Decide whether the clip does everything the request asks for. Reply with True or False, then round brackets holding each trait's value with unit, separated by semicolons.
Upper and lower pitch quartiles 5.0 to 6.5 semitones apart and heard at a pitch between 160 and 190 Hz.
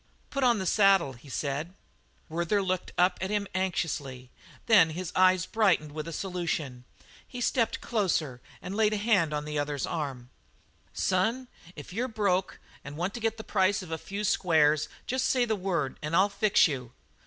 True (5.4 semitones; 185 Hz)